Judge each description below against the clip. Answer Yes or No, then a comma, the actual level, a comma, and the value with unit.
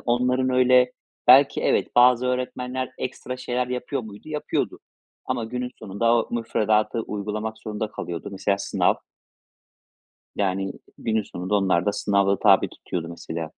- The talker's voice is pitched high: No, low, 115 Hz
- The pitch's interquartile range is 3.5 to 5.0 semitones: Yes, average, 3.9 semitones